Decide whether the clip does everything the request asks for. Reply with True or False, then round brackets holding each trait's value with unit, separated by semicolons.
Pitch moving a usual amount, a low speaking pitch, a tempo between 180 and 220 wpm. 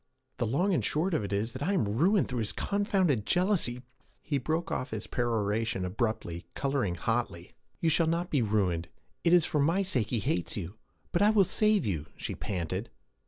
False (8.8 semitones; 125 Hz; 195 wpm)